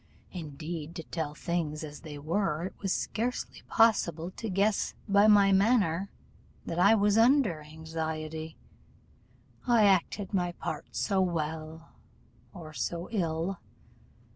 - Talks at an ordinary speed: No, slow, 130 wpm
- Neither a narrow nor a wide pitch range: Yes, average, 4.1 semitones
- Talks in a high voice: No, medium, 175 Hz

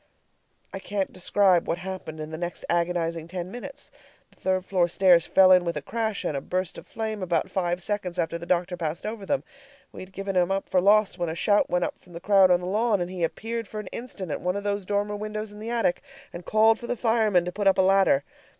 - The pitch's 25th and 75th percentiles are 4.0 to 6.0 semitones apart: No, average, 2.9 semitones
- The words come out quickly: Yes, fast, 250 wpm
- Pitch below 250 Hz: Yes, high, 190 Hz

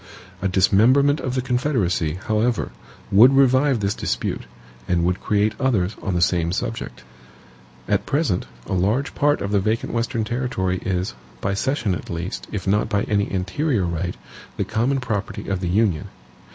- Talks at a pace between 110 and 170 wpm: Yes, average, 165 wpm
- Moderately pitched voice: No, low, 105 Hz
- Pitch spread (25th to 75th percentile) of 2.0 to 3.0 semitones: No, average, 5.2 semitones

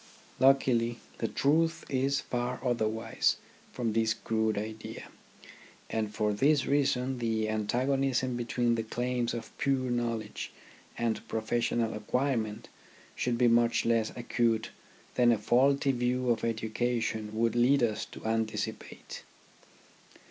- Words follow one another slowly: Yes, slow, 120 wpm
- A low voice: Yes, low, 120 Hz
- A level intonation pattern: Yes, narrow, 2.2 semitones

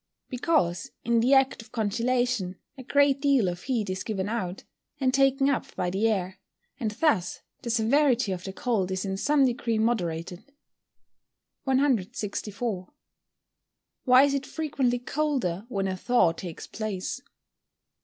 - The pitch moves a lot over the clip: Yes, wide, 5.7 semitones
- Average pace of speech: Yes, average, 145 wpm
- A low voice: No, high, 230 Hz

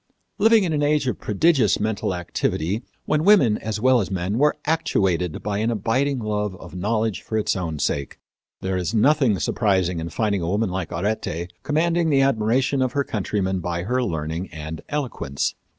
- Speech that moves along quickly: No, average, 180 wpm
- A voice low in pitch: Yes, low, 105 Hz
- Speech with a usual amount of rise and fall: No, wide, 6.5 semitones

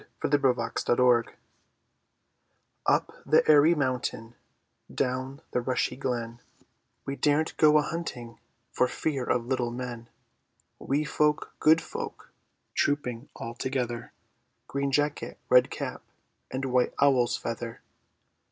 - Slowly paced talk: Yes, slow, 120 wpm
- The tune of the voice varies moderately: Yes, average, 3.1 semitones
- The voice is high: No, low, 130 Hz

